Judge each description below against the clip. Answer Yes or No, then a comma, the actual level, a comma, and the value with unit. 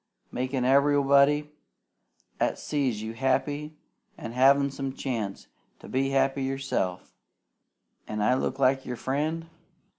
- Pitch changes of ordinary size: No, narrow, 1.7 semitones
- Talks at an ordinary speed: No, slow, 120 wpm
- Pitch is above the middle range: No, low, 135 Hz